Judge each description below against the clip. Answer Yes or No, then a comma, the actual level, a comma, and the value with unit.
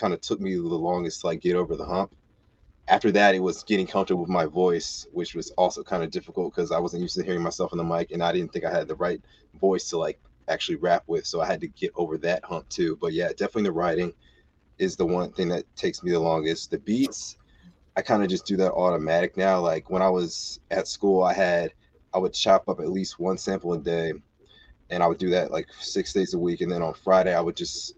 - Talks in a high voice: No, very low, 90 Hz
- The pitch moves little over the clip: Yes, narrow, 1.8 semitones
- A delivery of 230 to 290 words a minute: Yes, fast, 255 wpm